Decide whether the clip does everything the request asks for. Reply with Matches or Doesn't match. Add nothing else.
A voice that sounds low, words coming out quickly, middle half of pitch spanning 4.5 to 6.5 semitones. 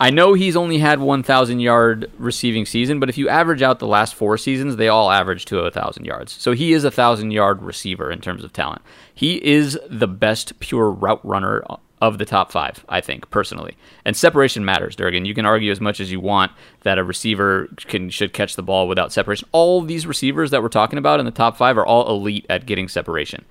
Matches